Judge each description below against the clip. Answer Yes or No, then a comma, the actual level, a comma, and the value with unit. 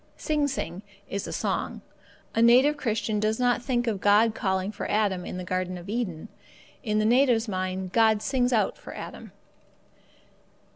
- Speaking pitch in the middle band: No, high, 215 Hz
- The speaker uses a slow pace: No, average, 165 wpm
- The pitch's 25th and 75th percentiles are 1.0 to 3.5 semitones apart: No, average, 4.2 semitones